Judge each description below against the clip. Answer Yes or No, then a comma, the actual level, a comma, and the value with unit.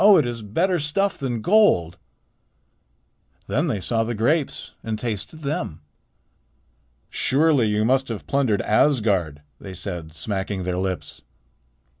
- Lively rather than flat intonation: Yes, wide, 7.2 semitones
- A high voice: No, low, 115 Hz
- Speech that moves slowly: Yes, slow, 125 wpm